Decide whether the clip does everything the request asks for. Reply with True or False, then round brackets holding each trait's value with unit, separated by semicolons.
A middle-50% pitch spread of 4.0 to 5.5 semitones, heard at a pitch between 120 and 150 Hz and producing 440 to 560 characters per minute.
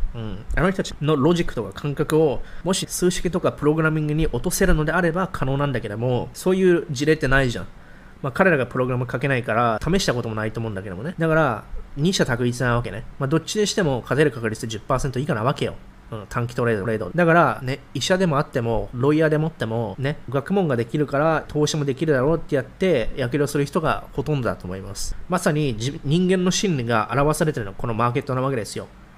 True (5.1 semitones; 140 Hz; 465 characters per minute)